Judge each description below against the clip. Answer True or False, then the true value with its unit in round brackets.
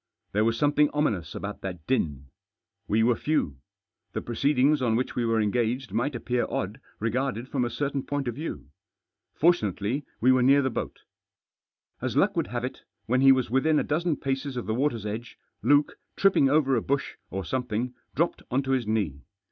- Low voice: True (125 Hz)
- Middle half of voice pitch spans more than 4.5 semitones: False (3.9 semitones)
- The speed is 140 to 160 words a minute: False (190 wpm)